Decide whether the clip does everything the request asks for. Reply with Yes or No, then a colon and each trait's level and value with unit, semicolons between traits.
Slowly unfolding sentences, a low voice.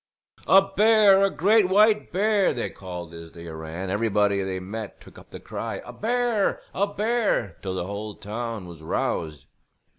No: average, 175 wpm; low, 110 Hz